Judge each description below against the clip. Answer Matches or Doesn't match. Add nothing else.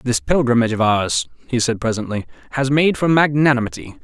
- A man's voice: Matches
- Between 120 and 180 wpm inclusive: Matches